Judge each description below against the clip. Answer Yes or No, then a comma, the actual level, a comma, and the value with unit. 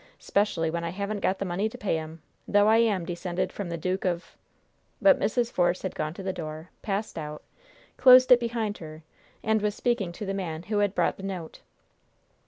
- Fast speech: Yes, fast, 210 wpm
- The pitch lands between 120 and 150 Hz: No, high, 190 Hz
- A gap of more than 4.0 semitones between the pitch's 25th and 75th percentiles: No, average, 3.7 semitones